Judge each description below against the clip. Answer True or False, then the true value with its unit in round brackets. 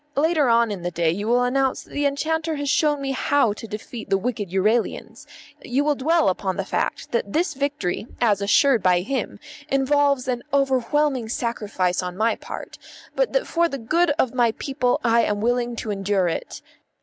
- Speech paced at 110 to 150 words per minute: False (190 wpm)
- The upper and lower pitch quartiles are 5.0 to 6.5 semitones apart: True (5.4 semitones)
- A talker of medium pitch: False (245 Hz)